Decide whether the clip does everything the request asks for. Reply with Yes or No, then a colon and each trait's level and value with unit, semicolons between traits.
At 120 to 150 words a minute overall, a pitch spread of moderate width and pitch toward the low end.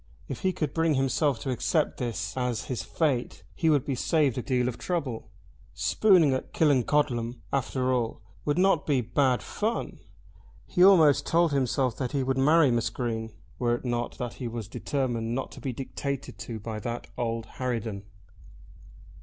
No: average, 170 wpm; average, 3.6 semitones; low, 130 Hz